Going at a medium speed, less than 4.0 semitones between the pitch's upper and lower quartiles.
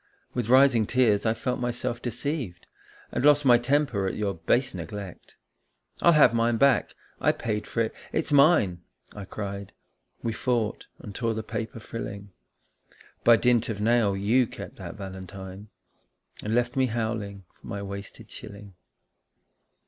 Yes: average, 155 wpm; average, 3.5 semitones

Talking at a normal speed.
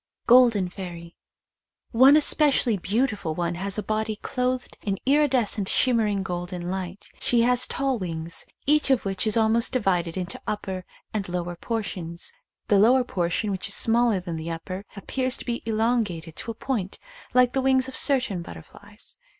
Yes: average, 165 wpm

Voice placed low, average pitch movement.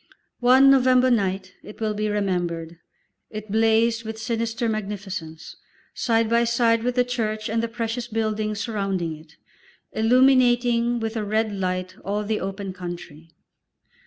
No: high, 220 Hz; average, 3.2 semitones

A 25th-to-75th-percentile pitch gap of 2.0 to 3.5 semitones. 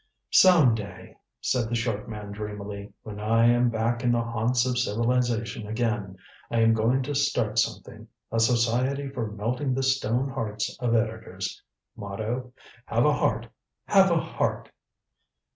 Yes: narrow, 2.5 semitones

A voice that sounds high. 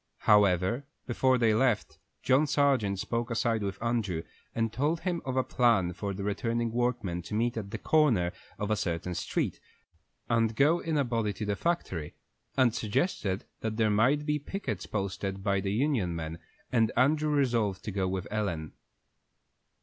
No: low, 110 Hz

